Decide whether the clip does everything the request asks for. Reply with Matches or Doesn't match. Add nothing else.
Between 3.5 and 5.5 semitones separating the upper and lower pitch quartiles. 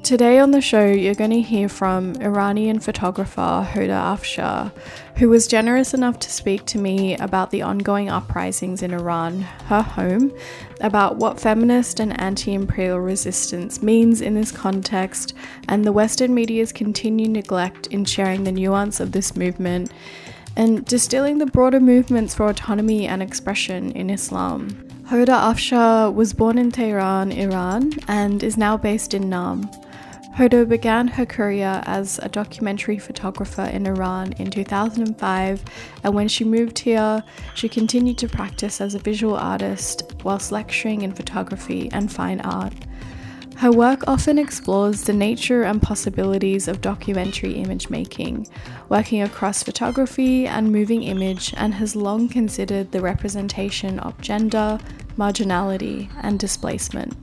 Doesn't match